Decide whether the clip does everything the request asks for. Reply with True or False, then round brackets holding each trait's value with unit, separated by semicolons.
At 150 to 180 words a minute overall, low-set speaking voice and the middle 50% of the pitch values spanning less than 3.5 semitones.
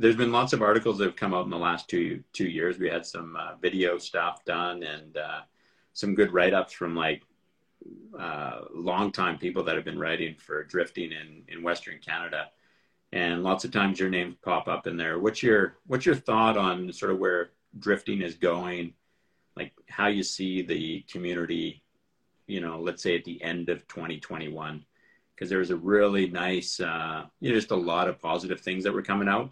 False (200 wpm; 90 Hz; 2.5 semitones)